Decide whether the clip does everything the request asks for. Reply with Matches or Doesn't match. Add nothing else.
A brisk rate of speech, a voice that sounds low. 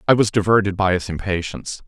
Doesn't match